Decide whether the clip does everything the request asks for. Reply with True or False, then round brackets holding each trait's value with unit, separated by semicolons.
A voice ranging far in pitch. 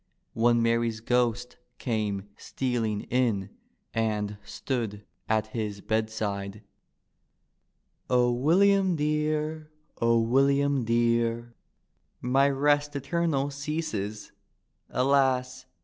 False (4.1 semitones)